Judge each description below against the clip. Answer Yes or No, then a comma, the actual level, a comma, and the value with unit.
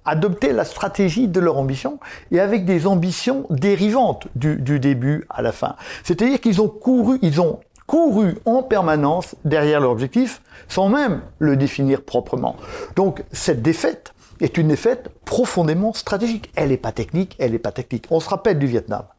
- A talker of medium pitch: Yes, medium, 175 Hz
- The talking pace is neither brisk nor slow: Yes, average, 170 wpm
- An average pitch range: No, wide, 7.1 semitones